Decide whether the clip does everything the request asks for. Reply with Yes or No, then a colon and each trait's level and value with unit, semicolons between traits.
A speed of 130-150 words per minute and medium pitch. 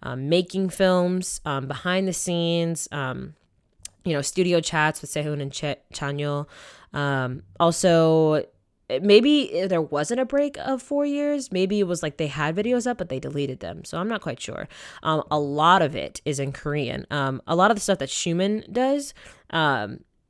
No: average, 185 wpm; medium, 165 Hz